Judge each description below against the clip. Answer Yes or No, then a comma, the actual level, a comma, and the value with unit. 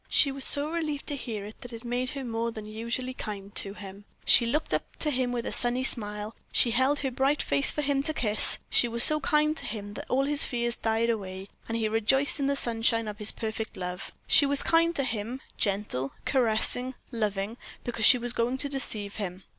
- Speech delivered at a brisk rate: Yes, fast, 220 wpm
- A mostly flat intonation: No, average, 4.2 semitones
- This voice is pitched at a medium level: No, high, 235 Hz